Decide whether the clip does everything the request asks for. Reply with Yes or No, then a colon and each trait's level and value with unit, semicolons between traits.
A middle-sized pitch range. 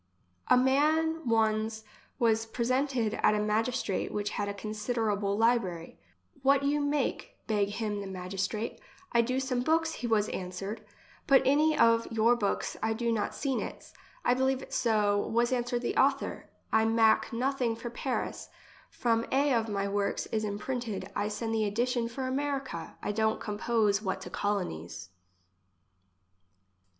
Yes: average, 3.7 semitones